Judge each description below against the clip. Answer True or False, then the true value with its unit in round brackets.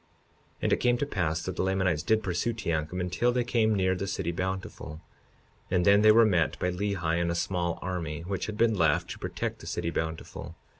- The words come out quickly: True (215 wpm)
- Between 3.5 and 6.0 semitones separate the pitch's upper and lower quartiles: True (3.8 semitones)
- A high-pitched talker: False (95 Hz)